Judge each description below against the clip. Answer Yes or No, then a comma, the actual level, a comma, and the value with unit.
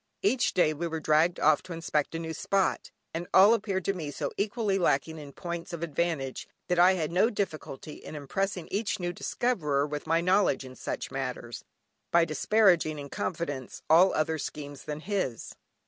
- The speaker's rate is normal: Yes, average, 180 wpm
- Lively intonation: No, average, 3.9 semitones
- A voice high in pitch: No, medium, 165 Hz